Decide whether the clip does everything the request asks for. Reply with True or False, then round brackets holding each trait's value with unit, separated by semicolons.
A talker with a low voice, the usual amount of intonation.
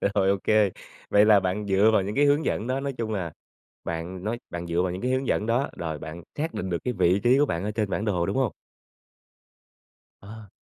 True (105 Hz; 4.5 semitones)